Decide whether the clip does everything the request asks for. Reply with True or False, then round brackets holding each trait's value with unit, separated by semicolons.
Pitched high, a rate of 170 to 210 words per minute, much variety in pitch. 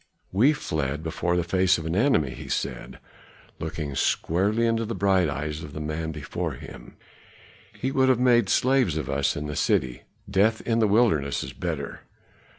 False (90 Hz; 175 wpm; 7.0 semitones)